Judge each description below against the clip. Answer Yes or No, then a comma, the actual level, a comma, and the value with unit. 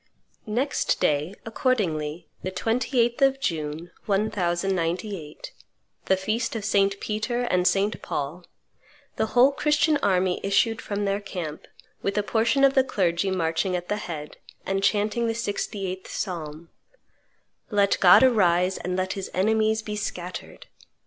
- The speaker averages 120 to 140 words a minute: Yes, slow, 135 wpm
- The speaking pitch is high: Yes, high, 200 Hz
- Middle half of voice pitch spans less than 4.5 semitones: Yes, average, 3.7 semitones